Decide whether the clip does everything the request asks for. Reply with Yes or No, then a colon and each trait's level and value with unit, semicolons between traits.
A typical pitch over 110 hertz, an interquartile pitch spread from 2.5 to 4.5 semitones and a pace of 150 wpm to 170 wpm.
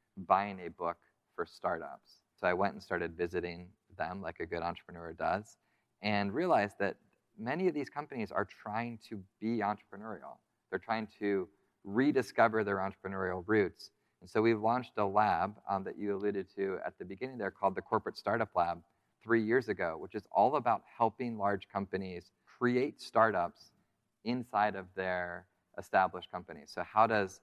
No: low, 100 Hz; average, 3.4 semitones; average, 165 wpm